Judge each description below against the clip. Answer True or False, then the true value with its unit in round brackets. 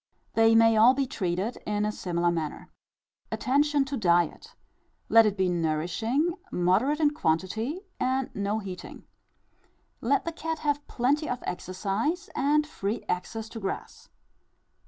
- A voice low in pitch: False (225 Hz)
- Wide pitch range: True (7.3 semitones)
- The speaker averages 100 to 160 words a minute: True (135 wpm)